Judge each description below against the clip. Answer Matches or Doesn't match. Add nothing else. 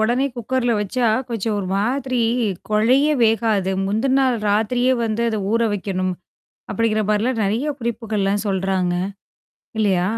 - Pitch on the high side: Matches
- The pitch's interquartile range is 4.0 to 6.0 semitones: Doesn't match